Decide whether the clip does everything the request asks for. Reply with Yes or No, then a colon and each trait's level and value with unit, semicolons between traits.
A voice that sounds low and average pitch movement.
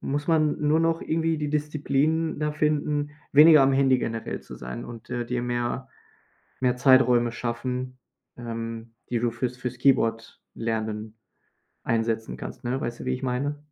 Yes: low, 125 Hz; average, 3.8 semitones